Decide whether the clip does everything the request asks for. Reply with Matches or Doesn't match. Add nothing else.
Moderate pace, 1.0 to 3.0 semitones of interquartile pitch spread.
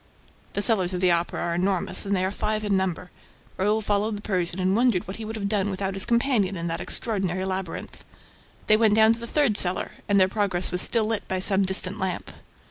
Doesn't match